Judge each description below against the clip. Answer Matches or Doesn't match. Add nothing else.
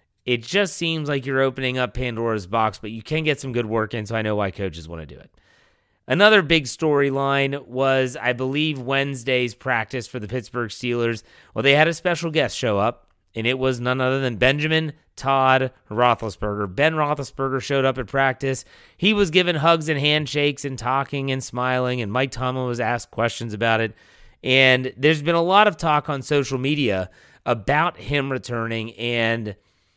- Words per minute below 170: Doesn't match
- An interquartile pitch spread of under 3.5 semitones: Doesn't match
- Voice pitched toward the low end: Matches